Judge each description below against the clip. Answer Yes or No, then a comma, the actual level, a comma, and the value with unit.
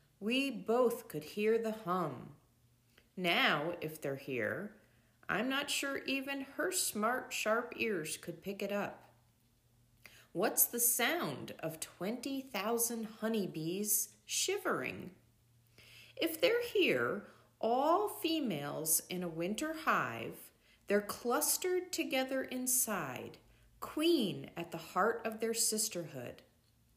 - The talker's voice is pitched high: Yes, high, 210 Hz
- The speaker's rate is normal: No, slow, 110 wpm